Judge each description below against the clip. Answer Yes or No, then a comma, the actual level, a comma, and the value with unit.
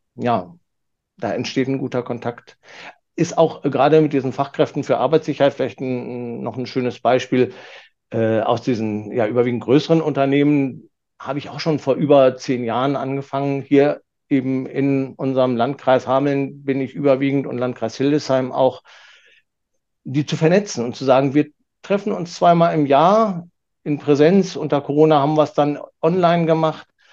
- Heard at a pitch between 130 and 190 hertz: Yes, medium, 140 Hz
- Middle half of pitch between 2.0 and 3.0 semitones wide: Yes, narrow, 2.6 semitones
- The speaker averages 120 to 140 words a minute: No, average, 155 wpm